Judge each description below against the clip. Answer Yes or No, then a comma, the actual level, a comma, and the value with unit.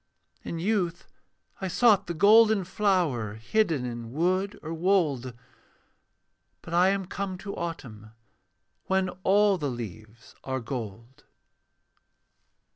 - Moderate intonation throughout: No, wide, 7.9 semitones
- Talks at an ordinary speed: No, slow, 115 wpm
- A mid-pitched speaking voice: Yes, medium, 170 Hz